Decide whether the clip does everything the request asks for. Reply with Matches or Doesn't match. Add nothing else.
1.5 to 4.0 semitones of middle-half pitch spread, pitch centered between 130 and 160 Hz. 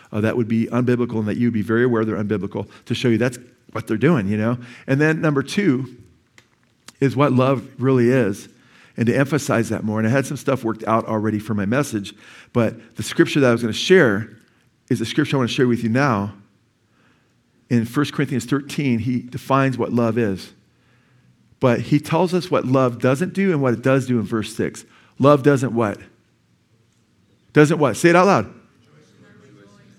Doesn't match